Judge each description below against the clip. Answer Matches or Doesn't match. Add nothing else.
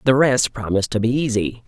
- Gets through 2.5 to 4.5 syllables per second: Doesn't match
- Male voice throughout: Matches